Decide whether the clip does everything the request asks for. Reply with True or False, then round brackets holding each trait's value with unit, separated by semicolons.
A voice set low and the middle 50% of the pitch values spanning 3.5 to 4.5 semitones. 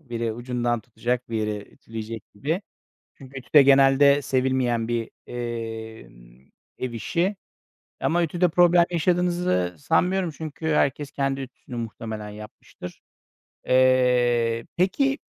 False (125 Hz; 4.9 semitones)